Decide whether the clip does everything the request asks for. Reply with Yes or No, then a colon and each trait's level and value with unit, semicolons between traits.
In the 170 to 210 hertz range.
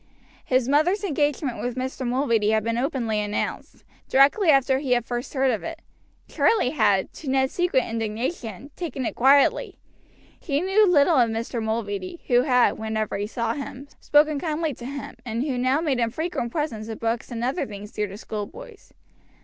No: very high, 255 Hz